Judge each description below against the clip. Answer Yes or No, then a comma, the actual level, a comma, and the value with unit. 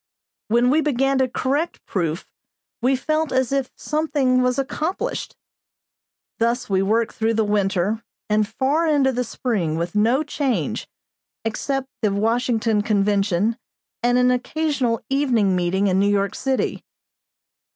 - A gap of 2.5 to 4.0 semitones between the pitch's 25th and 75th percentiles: No, average, 4.5 semitones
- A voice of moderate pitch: No, high, 240 Hz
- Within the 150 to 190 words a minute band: No, slow, 135 wpm